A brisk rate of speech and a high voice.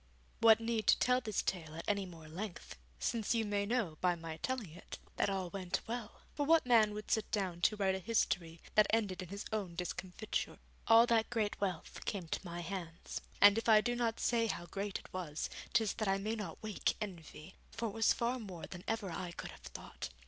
Yes: fast, 220 wpm; high, 205 Hz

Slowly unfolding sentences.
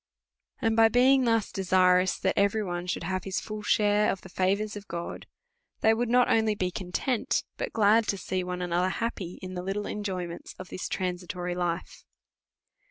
No: average, 185 wpm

